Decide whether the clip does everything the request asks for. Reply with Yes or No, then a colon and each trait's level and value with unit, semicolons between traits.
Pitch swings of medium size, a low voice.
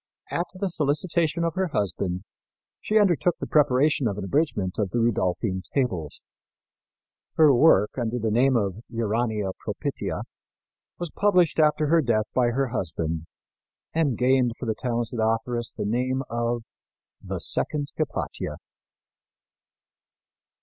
No: wide, 5.8 semitones; low, 120 Hz